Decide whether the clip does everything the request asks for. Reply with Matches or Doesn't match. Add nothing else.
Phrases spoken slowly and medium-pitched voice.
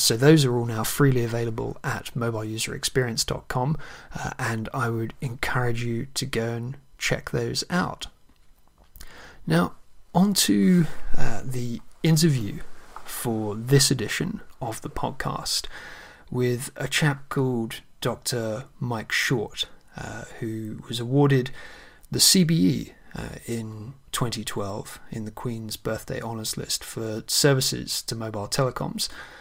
Doesn't match